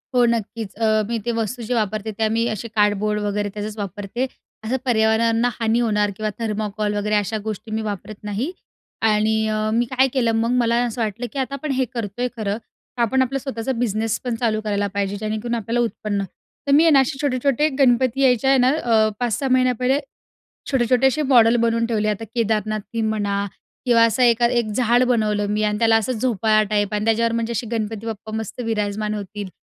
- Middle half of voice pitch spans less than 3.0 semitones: Yes, narrow, 2.4 semitones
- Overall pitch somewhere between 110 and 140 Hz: No, high, 225 Hz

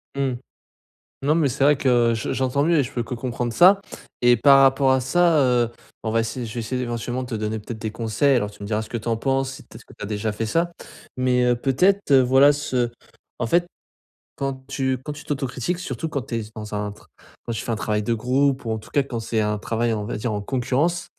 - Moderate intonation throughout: Yes, average, 3.4 semitones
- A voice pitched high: No, low, 125 Hz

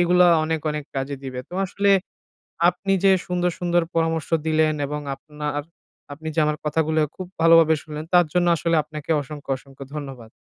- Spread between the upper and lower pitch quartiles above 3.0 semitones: No, narrow, 2.5 semitones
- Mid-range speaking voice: Yes, medium, 155 Hz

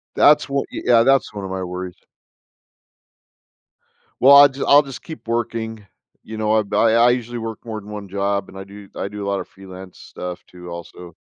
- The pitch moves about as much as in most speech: Yes, average, 3.6 semitones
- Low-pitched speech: Yes, low, 105 Hz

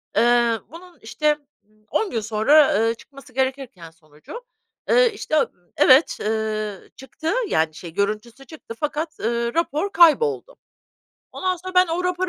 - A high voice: Yes, very high, 265 Hz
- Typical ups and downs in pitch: No, wide, 7.4 semitones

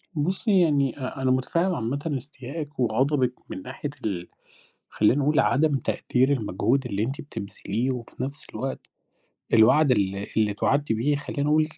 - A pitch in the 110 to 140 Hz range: Yes, low, 135 Hz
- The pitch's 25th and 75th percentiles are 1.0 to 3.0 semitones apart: No, average, 4.1 semitones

